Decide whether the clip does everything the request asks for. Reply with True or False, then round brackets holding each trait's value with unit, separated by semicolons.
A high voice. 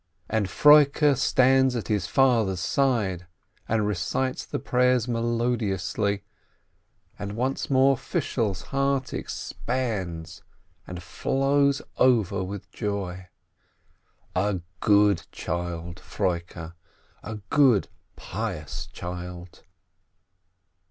False (105 Hz)